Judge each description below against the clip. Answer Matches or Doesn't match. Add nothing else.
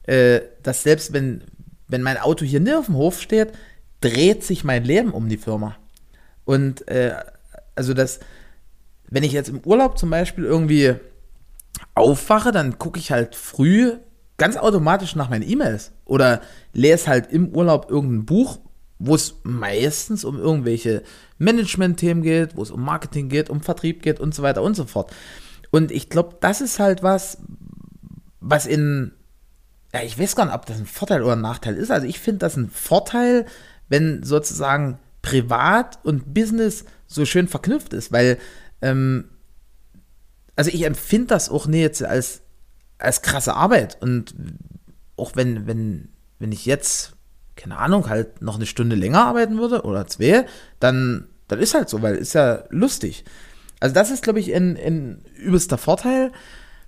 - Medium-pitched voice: Matches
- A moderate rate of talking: Matches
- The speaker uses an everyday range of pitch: Doesn't match